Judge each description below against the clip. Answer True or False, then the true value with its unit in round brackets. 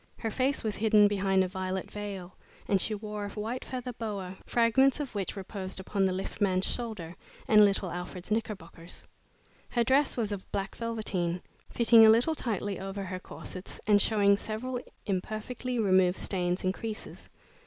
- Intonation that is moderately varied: True (3.2 semitones)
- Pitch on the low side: False (205 Hz)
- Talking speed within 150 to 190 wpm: True (165 wpm)